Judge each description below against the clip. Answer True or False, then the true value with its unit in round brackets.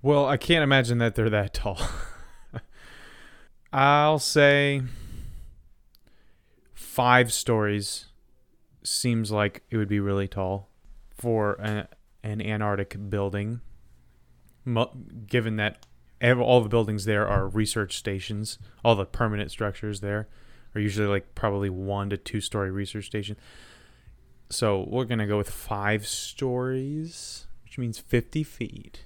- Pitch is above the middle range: False (105 Hz)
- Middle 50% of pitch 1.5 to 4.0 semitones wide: True (3.0 semitones)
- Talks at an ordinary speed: False (125 wpm)